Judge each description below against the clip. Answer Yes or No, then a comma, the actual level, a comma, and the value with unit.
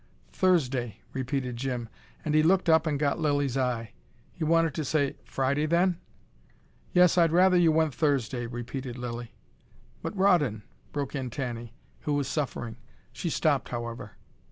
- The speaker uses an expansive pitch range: No, average, 4.6 semitones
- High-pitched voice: No, medium, 140 Hz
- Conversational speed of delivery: Yes, average, 155 wpm